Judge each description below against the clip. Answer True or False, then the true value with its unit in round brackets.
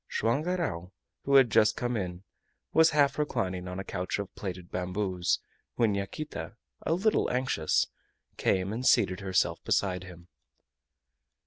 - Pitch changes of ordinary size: False (5.9 semitones)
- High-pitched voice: False (100 Hz)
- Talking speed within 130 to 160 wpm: True (140 wpm)